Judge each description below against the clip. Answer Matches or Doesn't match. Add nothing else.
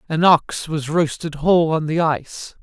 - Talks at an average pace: Matches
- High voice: Doesn't match